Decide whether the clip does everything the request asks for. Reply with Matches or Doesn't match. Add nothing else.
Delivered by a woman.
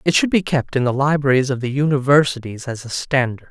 Doesn't match